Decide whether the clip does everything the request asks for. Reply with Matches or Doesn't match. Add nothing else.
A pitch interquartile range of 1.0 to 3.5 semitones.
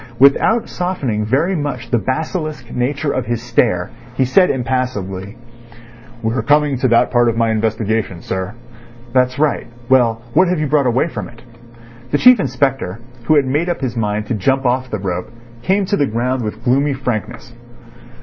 Doesn't match